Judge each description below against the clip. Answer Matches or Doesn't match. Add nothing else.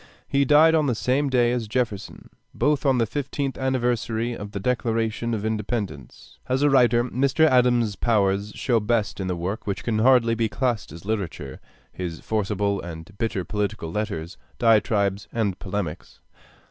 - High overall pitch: Doesn't match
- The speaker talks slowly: Doesn't match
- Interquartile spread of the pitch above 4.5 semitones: Doesn't match